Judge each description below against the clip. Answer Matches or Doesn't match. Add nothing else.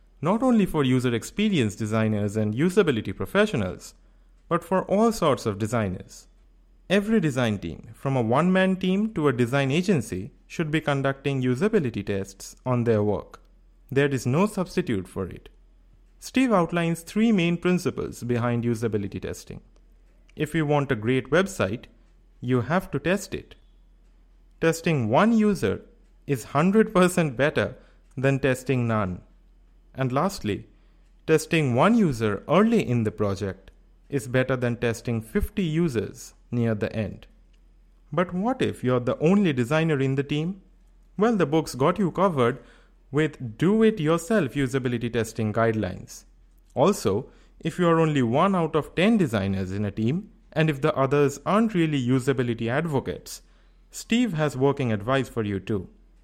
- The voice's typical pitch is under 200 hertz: Matches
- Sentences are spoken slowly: Doesn't match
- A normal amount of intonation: Doesn't match